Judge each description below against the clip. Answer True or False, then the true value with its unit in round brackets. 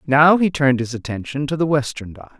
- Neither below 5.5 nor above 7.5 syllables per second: True (5.8 syllables/s)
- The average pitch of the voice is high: False (140 Hz)